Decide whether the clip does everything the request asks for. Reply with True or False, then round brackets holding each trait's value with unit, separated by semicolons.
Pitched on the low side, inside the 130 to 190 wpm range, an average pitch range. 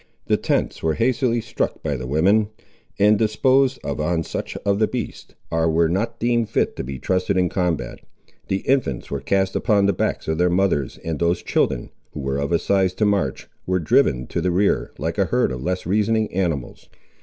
False (90 Hz; 200 wpm; 4.8 semitones)